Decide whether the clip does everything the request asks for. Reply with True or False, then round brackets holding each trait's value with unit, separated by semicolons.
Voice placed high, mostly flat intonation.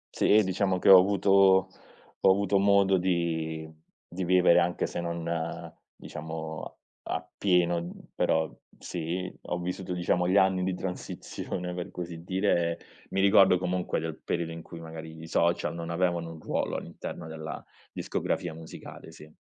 False (90 Hz; 2.0 semitones)